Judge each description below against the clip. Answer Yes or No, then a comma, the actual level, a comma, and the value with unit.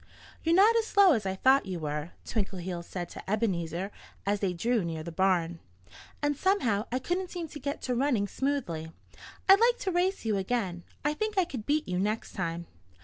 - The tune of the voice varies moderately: No, wide, 8.9 semitones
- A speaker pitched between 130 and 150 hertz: No, high, 220 Hz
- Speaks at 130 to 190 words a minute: No, average, 200 wpm